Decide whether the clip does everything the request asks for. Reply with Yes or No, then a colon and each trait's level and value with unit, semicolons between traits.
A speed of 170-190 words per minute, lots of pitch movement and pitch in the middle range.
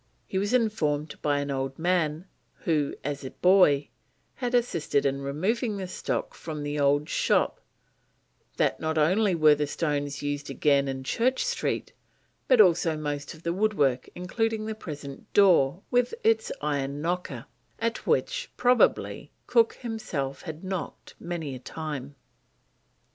No: average, 145 wpm; wide, 6.3 semitones; medium, 160 Hz